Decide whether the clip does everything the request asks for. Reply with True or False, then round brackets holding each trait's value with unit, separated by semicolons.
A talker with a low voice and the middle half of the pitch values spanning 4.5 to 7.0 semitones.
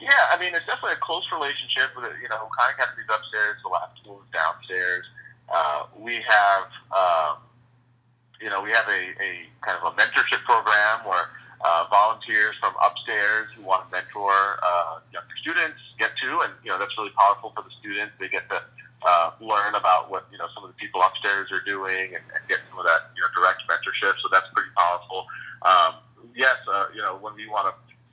True (115 Hz; 4.9 semitones)